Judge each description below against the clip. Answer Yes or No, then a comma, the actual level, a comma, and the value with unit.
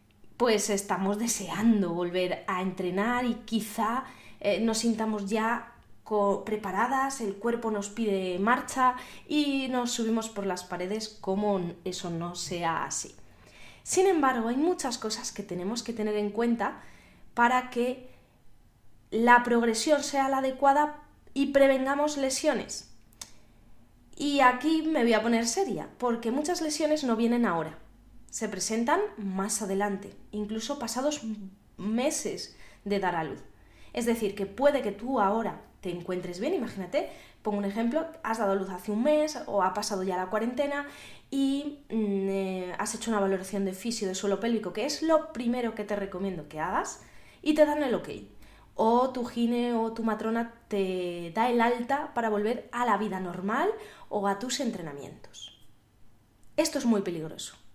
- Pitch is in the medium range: No, high, 220 Hz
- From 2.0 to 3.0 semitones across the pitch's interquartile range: No, average, 4.5 semitones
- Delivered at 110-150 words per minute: No, average, 160 wpm